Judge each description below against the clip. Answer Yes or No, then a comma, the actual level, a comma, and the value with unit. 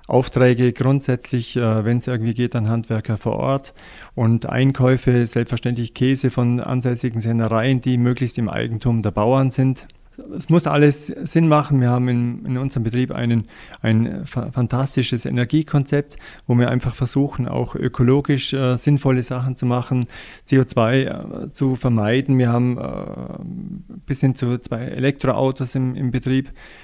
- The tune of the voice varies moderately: No, narrow, 1.9 semitones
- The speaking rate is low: No, average, 140 wpm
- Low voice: Yes, low, 125 Hz